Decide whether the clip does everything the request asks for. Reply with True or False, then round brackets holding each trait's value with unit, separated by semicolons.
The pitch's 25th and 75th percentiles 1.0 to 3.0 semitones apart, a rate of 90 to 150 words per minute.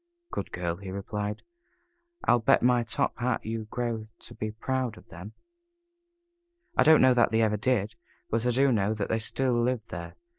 False (2.7 semitones; 185 wpm)